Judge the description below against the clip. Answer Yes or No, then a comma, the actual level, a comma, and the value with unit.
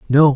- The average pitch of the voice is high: No, medium, 140 Hz